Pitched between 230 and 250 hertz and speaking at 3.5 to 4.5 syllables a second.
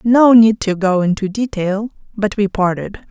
No: high, 205 Hz; 4.4 syllables/s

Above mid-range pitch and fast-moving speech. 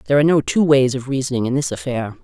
No: low, 135 Hz; fast, 270 wpm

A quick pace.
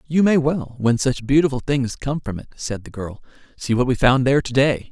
Yes: fast, 245 wpm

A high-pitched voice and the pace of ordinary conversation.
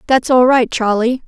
Yes: high, 245 Hz; average, 190 wpm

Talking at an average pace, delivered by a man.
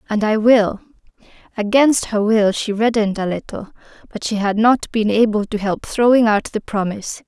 No: average, 180 wpm; female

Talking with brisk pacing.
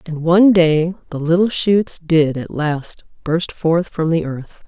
No: average, 180 wpm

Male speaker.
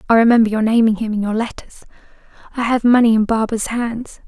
No: female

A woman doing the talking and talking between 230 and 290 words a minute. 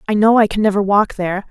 Yes: female; fast, 280 wpm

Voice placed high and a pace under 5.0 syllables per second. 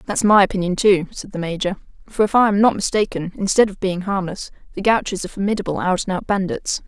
No: high, 195 Hz; 6.2 syllables/s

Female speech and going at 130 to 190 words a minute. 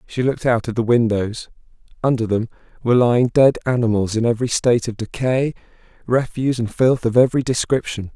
No: male; average, 170 wpm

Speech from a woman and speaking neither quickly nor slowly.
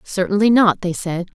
Yes: female; average, 175 wpm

